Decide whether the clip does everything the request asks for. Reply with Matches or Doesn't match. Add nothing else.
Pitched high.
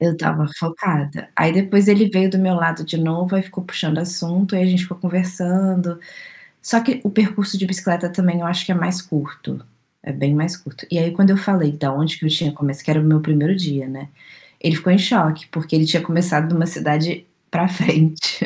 Doesn't match